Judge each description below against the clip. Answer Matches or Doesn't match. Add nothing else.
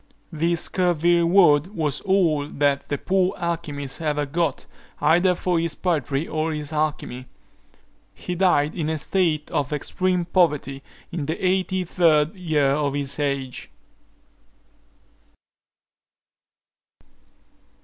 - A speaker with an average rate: Doesn't match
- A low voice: Doesn't match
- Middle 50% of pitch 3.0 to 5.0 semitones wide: Matches